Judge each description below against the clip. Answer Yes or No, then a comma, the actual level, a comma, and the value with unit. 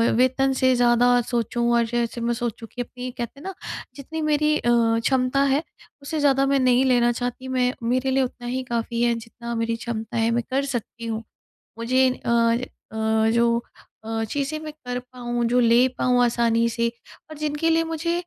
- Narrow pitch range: Yes, narrow, 2.3 semitones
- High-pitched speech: Yes, high, 245 Hz